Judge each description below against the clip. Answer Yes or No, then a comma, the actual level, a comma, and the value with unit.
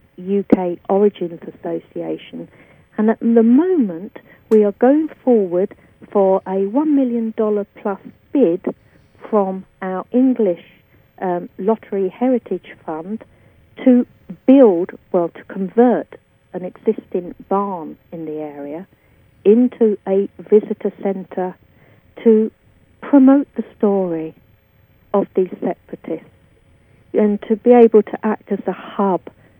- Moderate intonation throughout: Yes, average, 3.9 semitones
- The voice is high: Yes, high, 200 Hz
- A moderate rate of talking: No, slow, 110 wpm